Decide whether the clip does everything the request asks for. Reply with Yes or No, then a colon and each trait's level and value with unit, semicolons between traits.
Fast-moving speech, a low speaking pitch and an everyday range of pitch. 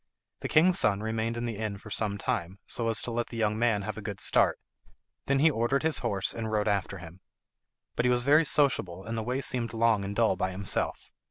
Yes: fast, 235 wpm; low, 110 Hz; average, 3.1 semitones